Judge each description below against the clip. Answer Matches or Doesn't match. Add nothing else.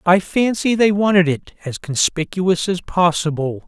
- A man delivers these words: Matches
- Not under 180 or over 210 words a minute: Doesn't match